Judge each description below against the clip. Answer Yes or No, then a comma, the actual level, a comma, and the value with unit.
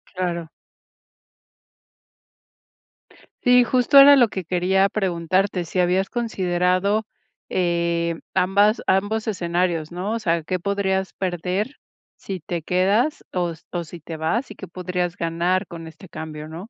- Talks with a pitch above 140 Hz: Yes, medium, 185 Hz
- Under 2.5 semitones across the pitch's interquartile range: No, average, 2.8 semitones